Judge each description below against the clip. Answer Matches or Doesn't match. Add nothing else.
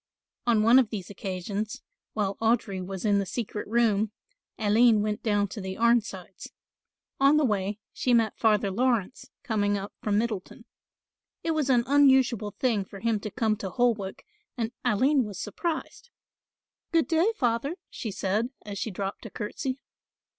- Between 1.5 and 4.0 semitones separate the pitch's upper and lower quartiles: Matches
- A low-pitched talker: Doesn't match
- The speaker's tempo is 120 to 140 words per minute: Doesn't match